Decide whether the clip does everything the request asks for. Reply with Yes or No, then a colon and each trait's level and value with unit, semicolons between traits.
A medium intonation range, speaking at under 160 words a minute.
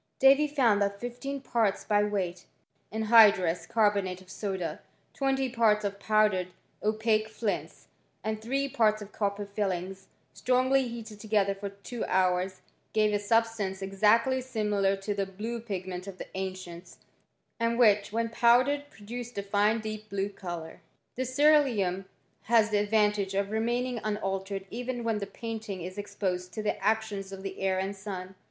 No: average, 3.0 semitones; average, 165 wpm